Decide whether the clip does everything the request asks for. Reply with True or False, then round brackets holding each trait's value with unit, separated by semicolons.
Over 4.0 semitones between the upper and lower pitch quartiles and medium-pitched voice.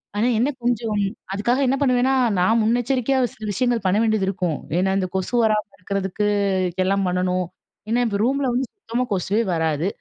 False (4.4 semitones; 215 Hz)